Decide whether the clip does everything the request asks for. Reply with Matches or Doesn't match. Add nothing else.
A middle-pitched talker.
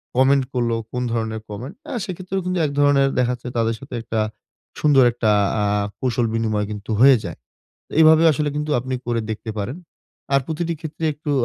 Doesn't match